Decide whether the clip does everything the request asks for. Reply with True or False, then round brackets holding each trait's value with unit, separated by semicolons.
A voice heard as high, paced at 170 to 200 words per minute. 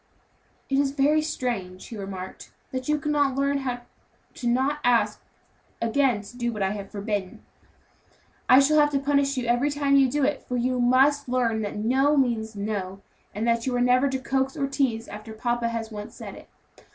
True (250 Hz; 190 wpm)